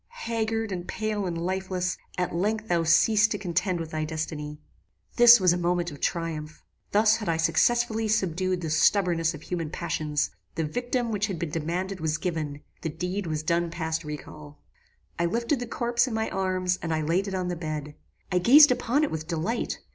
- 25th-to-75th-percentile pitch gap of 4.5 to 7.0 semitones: Yes, average, 4.9 semitones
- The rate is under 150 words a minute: No, average, 190 wpm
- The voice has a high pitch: No, medium, 180 Hz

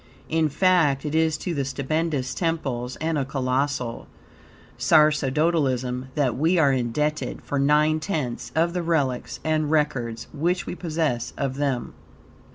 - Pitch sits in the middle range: Yes, medium, 150 Hz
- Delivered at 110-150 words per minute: Yes, average, 140 wpm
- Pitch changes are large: No, average, 3.5 semitones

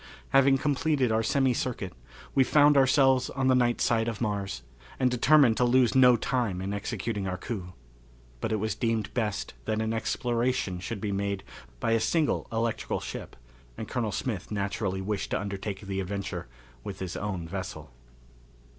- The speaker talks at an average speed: Yes, average, 170 wpm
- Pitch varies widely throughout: No, average, 4.2 semitones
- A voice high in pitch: No, low, 110 Hz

